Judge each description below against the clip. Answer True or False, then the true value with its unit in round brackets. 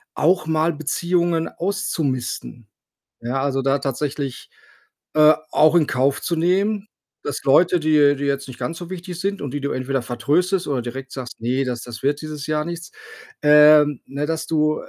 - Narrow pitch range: False (3.6 semitones)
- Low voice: False (150 Hz)